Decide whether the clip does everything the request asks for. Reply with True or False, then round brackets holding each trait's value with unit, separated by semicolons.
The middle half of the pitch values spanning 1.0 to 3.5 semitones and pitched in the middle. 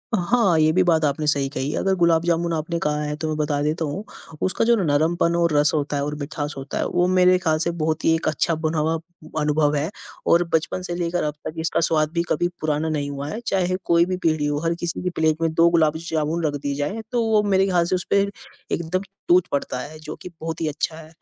True (2.5 semitones; 160 Hz)